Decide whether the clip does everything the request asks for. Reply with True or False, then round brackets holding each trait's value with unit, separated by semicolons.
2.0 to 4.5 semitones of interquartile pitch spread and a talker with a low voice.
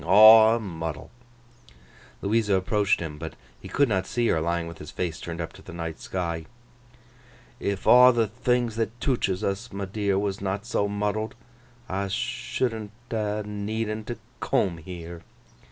True (4.2 semitones; 100 Hz)